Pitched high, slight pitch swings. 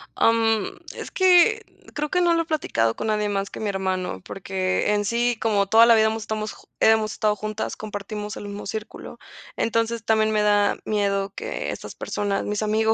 Yes: high, 215 Hz; narrow, 1.8 semitones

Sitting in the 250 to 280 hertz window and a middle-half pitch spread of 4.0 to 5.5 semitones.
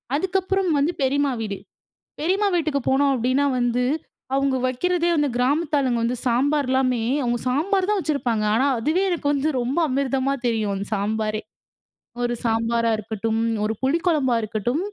Yes: very high, 265 Hz; average, 4.5 semitones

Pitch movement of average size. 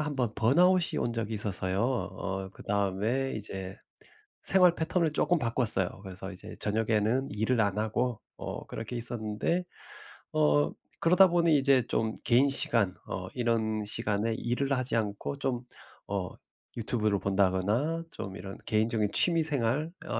Yes: average, 4.8 semitones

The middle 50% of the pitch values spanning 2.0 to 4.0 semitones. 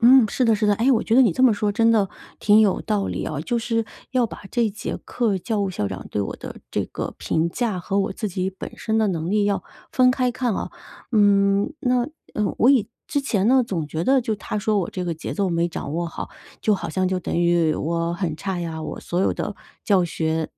No: average, 4.9 semitones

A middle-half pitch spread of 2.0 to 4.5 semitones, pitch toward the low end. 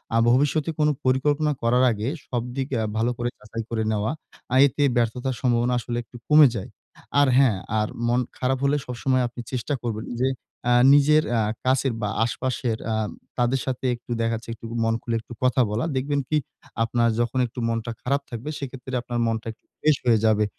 Yes: narrow, 2.5 semitones; low, 125 Hz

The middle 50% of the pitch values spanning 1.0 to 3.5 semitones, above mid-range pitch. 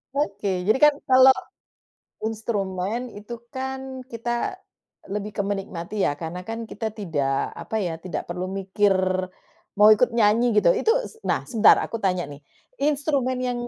No: average, 4.5 semitones; high, 215 Hz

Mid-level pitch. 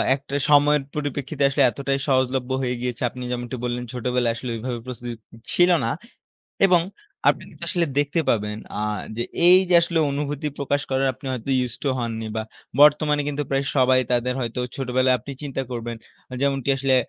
No: low, 130 Hz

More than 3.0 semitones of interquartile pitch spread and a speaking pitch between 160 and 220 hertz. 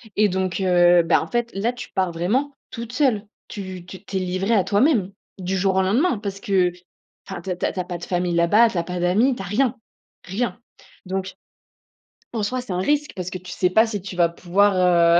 Yes: average, 3.6 semitones; high, 190 Hz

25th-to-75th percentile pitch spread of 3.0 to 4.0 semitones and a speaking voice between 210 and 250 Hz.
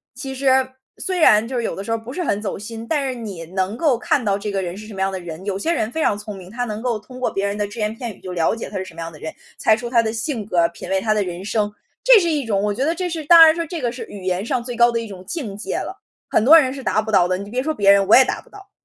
No: average, 4.7 semitones; high, 220 Hz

